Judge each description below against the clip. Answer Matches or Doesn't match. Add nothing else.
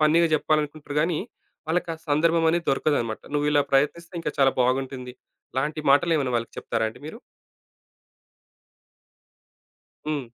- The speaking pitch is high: Doesn't match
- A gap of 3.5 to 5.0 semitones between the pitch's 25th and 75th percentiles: Doesn't match